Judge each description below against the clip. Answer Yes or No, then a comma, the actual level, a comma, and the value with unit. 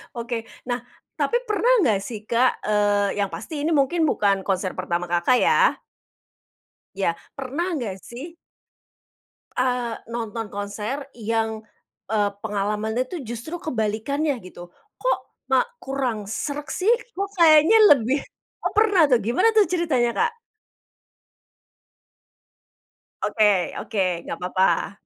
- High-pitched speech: Yes, high, 240 Hz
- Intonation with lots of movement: Yes, wide, 6.9 semitones